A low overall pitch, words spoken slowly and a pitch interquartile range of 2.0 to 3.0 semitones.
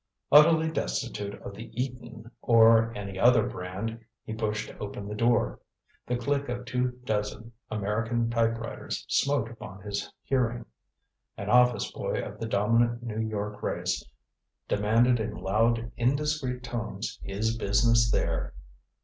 Yes: low, 115 Hz; slow, 130 wpm; narrow, 2.6 semitones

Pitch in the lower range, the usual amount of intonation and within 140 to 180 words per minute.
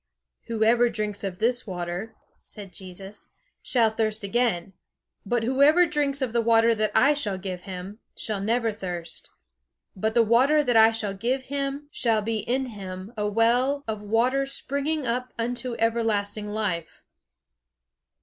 No: high, 225 Hz; average, 3.5 semitones; average, 150 wpm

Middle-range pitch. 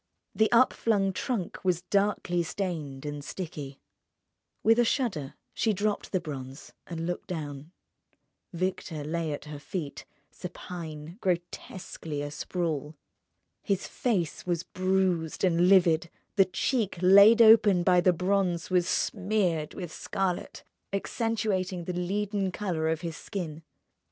Yes: medium, 180 Hz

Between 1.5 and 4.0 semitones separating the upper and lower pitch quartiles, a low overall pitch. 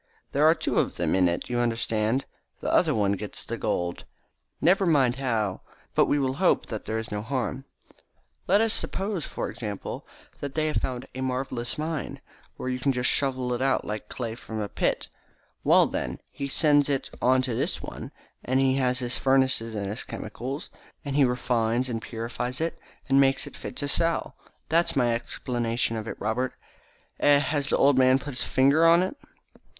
Yes: average, 3.5 semitones; low, 130 Hz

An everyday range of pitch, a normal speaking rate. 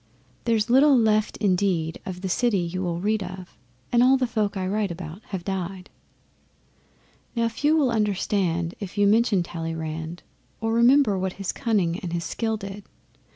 Yes: average, 4.1 semitones; average, 165 wpm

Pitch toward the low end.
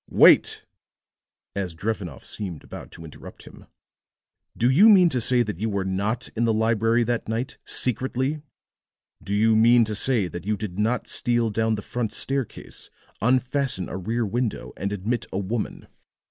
Yes: low, 110 Hz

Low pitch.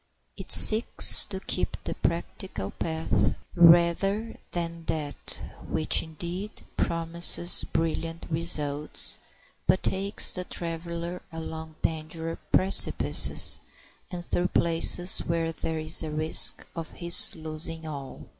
No: medium, 165 Hz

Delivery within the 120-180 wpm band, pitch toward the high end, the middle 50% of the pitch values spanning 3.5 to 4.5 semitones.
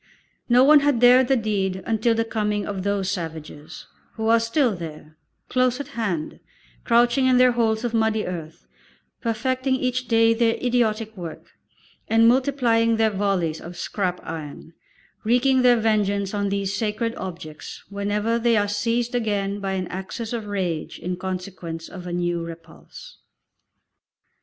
Yes: average, 150 wpm; high, 215 Hz; average, 4.1 semitones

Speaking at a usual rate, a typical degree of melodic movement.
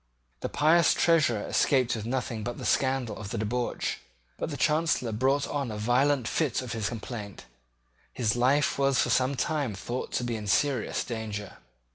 Yes: average, 175 wpm; average, 4.0 semitones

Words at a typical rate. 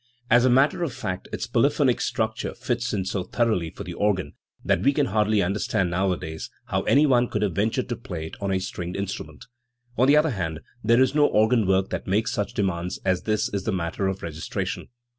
No: fast, 210 wpm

